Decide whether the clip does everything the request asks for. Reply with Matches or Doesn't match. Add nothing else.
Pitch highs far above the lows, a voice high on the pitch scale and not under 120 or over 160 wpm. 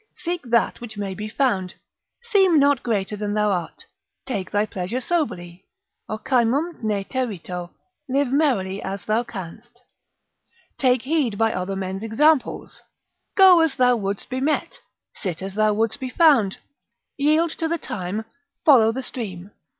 Matches